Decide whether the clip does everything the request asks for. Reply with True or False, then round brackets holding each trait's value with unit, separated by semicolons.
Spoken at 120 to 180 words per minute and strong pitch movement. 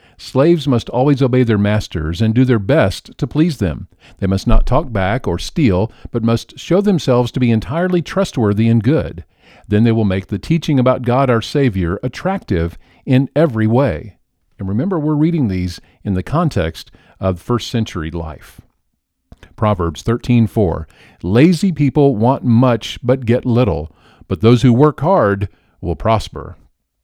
True (160 wpm; 6.3 semitones)